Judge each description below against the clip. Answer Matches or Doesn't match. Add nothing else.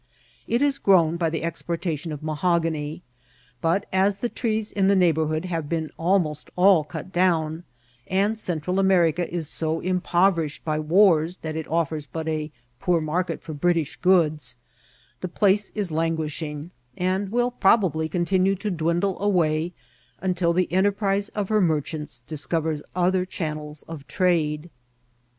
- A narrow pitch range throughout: Doesn't match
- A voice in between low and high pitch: Matches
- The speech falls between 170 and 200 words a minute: Doesn't match